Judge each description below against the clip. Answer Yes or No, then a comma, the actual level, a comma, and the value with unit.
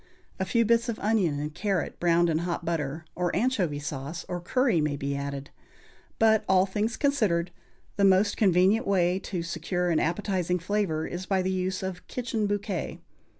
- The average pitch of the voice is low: No, medium, 180 Hz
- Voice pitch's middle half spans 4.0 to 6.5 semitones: No, average, 3.6 semitones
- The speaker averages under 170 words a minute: No, average, 175 wpm